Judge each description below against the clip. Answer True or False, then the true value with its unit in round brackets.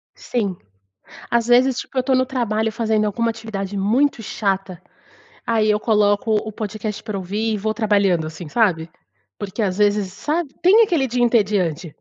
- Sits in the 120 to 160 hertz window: False (215 Hz)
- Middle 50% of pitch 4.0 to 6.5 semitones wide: False (3.1 semitones)